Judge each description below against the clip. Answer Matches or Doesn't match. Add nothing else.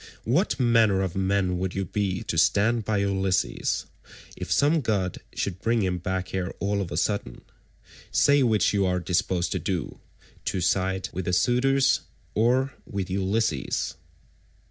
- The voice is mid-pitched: Doesn't match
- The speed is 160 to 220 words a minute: Doesn't match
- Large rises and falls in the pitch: Doesn't match